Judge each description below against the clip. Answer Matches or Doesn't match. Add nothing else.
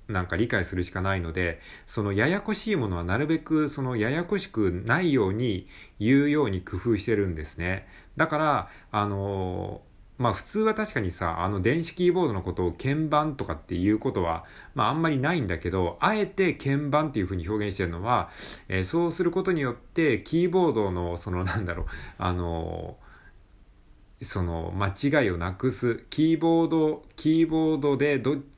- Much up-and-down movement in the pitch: Matches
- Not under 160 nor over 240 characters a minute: Doesn't match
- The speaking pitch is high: Doesn't match